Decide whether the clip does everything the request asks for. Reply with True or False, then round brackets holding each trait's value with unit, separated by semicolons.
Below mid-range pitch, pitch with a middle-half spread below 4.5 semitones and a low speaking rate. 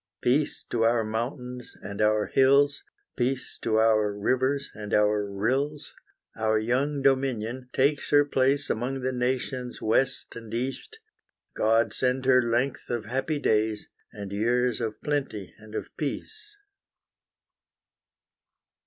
True (125 Hz; 3.5 semitones; 125 wpm)